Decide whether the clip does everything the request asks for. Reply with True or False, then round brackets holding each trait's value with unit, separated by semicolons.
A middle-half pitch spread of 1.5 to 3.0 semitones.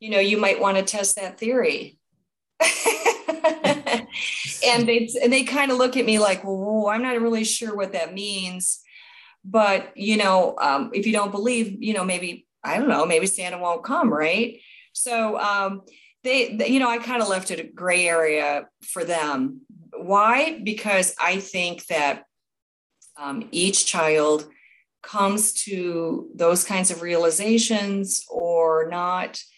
False (4.4 semitones)